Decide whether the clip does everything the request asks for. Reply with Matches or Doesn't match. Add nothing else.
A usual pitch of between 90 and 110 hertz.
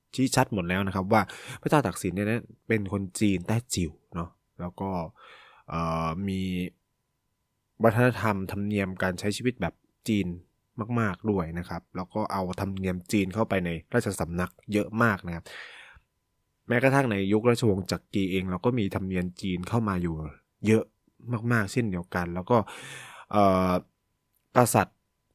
Matches